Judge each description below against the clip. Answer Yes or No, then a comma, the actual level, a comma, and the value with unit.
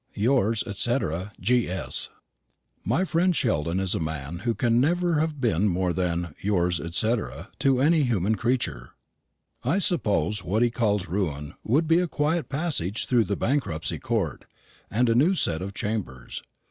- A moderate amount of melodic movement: No, wide, 7.5 semitones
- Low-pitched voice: Yes, low, 110 Hz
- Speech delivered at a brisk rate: No, average, 160 wpm